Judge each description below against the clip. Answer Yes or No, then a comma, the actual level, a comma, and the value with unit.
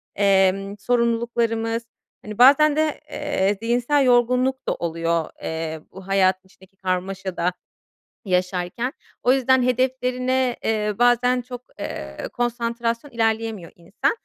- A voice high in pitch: Yes, high, 230 Hz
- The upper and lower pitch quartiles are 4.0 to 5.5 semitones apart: Yes, average, 4.7 semitones